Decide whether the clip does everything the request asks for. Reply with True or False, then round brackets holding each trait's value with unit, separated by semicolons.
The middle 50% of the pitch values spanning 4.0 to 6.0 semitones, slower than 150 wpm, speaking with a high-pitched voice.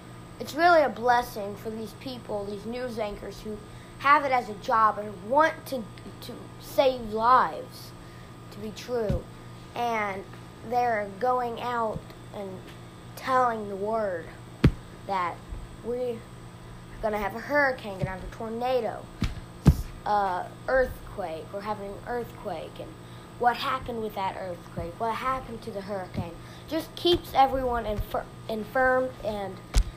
False (3.6 semitones; 135 wpm; 230 Hz)